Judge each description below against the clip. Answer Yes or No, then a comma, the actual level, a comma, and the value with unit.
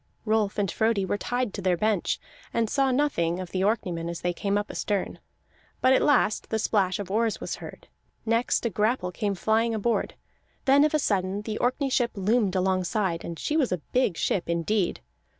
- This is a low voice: No, high, 210 Hz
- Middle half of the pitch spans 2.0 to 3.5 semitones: No, average, 3.9 semitones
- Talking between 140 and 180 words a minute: No, average, 195 wpm